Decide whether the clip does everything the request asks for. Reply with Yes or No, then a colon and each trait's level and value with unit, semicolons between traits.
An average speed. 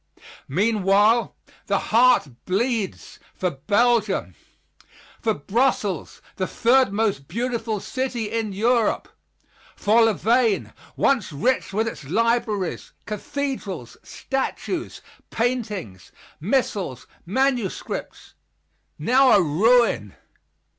No: slow, 85 wpm